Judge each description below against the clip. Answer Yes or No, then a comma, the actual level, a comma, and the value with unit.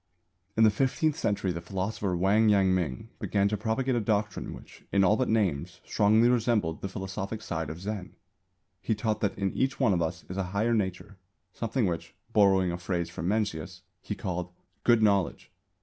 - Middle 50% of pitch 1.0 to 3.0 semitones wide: No, average, 3.4 semitones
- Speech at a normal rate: Yes, average, 185 wpm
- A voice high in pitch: No, low, 100 Hz